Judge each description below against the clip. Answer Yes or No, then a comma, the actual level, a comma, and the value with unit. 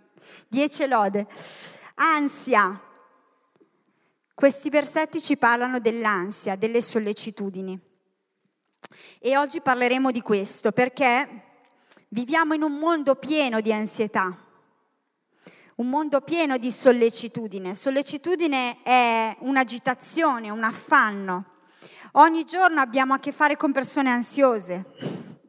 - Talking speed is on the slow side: Yes, slow, 100 wpm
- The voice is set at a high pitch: Yes, very high, 250 Hz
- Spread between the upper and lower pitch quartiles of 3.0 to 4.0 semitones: No, average, 4.5 semitones